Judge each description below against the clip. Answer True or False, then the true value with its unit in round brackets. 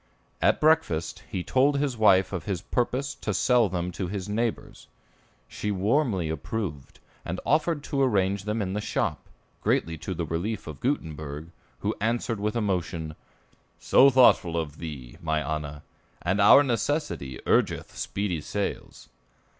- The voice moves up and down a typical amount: False (6.3 semitones)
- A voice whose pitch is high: False (100 Hz)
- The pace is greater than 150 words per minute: False (145 wpm)